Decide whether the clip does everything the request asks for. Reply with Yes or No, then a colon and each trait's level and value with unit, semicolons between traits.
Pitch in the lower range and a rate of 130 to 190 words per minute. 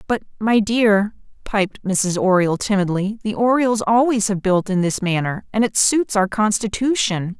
No: high, 205 Hz; average, 160 wpm